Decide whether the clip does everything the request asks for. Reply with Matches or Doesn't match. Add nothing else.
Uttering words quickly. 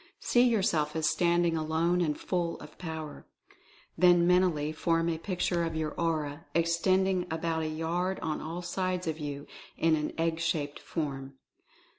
Doesn't match